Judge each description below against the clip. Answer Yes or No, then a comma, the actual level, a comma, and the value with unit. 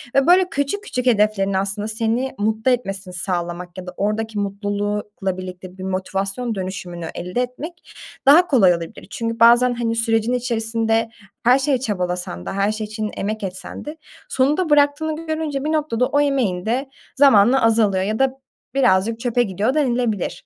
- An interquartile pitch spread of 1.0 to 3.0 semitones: No, average, 4.9 semitones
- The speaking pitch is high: Yes, high, 225 Hz